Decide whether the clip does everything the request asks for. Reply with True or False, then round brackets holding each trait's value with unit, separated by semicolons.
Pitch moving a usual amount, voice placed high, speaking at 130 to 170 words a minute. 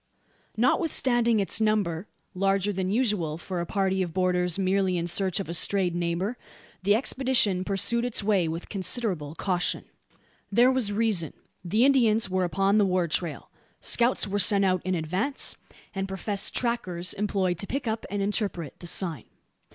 True (3.3 semitones; 195 Hz; 160 wpm)